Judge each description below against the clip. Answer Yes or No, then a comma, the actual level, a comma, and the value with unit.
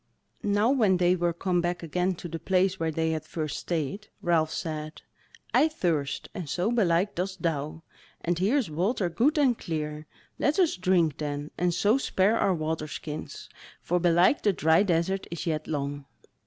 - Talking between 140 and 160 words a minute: No, average, 180 wpm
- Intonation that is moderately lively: Yes, average, 3.4 semitones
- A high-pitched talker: No, medium, 175 Hz